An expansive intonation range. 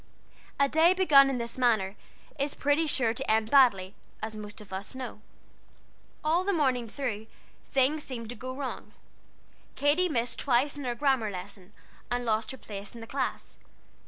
No: average, 4.4 semitones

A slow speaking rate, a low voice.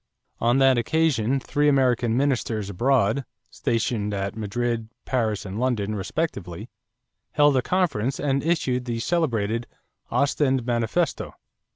Yes: slow, 115 wpm; low, 120 Hz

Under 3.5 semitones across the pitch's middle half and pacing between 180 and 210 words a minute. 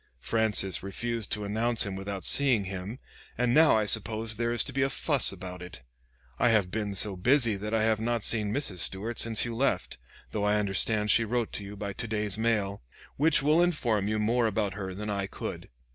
Yes: average, 2.8 semitones; fast, 205 wpm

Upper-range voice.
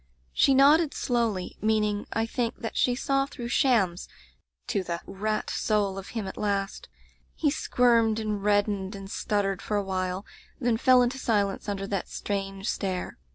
Yes: high, 210 Hz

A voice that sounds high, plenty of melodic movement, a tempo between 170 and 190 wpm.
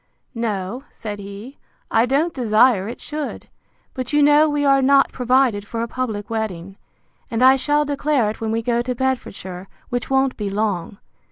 No: high, 240 Hz; average, 4.3 semitones; average, 175 wpm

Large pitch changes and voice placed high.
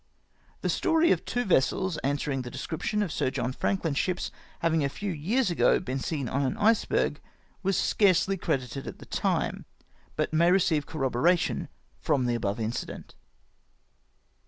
No: wide, 5.8 semitones; medium, 160 Hz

